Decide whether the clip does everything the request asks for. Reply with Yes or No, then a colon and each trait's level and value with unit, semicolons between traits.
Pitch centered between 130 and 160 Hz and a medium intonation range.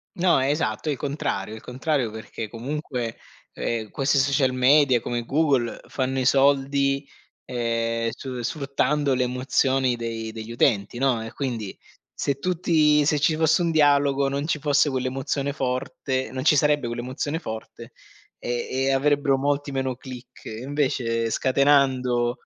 Yes: low, 135 Hz; average, 3.0 semitones